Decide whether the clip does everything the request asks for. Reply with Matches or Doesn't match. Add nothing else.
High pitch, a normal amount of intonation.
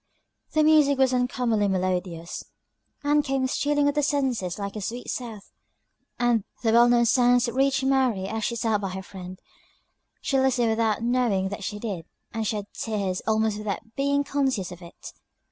Matches